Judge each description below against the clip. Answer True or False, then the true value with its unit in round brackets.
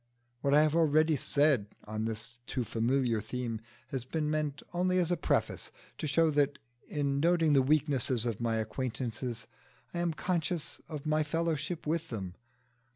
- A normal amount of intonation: True (4.6 semitones)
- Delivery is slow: False (160 wpm)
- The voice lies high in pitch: False (145 Hz)